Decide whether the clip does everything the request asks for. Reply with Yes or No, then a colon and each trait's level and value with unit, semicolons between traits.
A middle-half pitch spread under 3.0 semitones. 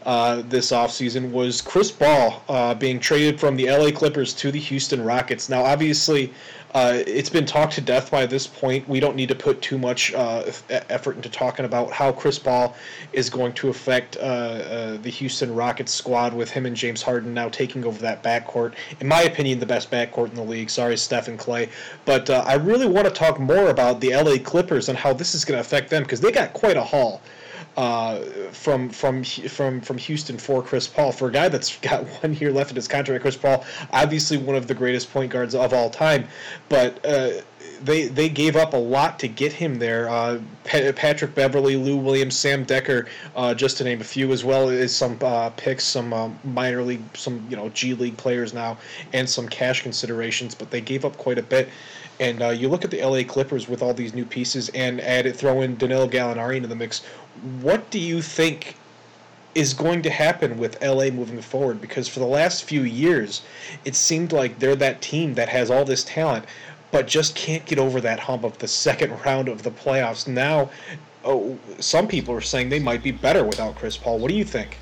Yes: narrow, 2.4 semitones